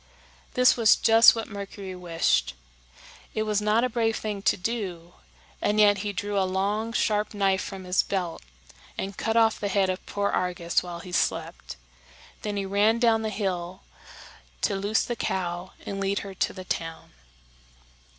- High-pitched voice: Yes, high, 200 Hz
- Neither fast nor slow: Yes, average, 170 wpm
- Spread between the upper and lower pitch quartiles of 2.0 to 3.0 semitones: Yes, narrow, 2.6 semitones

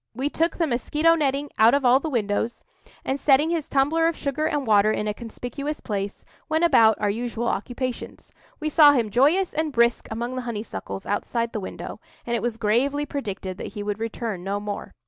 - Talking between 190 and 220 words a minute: Yes, average, 200 wpm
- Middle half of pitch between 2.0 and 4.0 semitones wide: No, average, 5.0 semitones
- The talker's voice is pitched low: No, high, 245 Hz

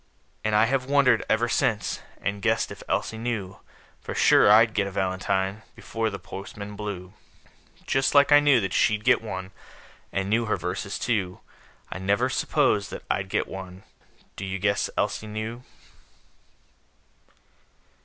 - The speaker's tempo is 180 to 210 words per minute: No, average, 155 wpm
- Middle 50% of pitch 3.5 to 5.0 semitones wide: No, average, 2.9 semitones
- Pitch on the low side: Yes, low, 105 Hz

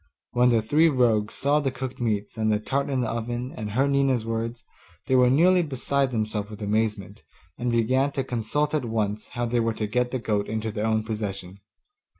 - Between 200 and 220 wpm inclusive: Yes, fast, 205 wpm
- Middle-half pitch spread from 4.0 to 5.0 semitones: No, average, 3.4 semitones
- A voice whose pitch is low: Yes, low, 115 Hz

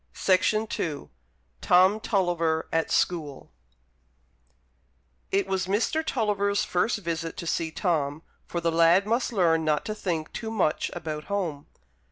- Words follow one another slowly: Yes, slow, 130 wpm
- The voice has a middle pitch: Yes, medium, 180 Hz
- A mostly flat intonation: No, average, 3.7 semitones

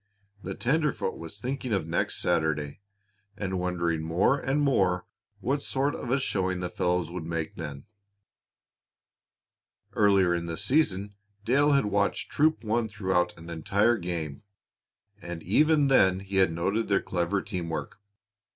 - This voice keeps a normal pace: Yes, average, 145 wpm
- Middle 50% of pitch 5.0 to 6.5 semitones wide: Yes, wide, 5.6 semitones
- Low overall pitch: Yes, very low, 95 Hz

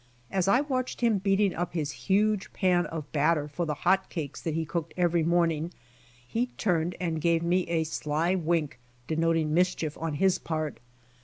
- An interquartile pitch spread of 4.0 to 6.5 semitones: No, average, 2.8 semitones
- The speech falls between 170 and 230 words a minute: Yes, average, 180 wpm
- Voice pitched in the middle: Yes, medium, 170 Hz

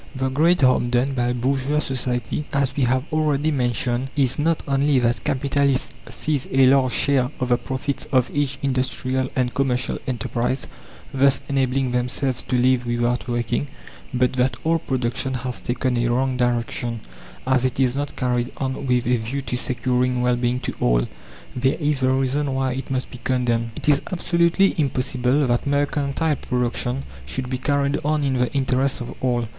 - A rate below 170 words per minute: No, average, 175 wpm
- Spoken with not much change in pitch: Yes, narrow, 2.0 semitones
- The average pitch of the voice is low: Yes, low, 130 Hz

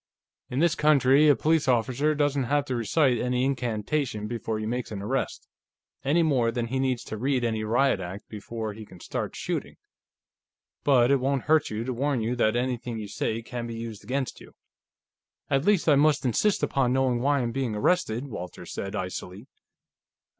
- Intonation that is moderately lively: Yes, average, 3.8 semitones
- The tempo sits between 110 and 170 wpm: No, average, 185 wpm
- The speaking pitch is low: Yes, low, 125 Hz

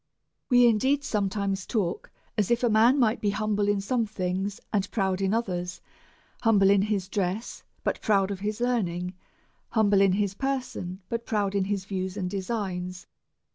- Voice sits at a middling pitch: No, high, 200 Hz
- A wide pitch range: No, average, 2.7 semitones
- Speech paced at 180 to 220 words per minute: No, average, 170 wpm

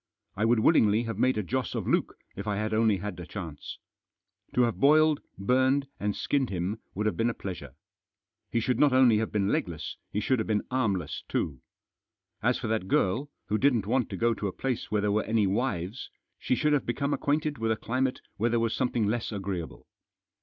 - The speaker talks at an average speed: No, fast, 210 wpm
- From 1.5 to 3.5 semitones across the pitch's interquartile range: No, average, 4.0 semitones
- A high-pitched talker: No, low, 110 Hz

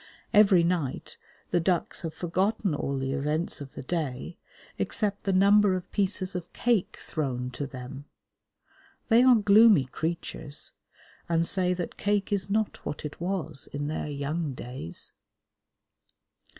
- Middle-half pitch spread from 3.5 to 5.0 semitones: No, wide, 5.5 semitones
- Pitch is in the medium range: Yes, medium, 170 Hz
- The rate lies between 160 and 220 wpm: No, average, 140 wpm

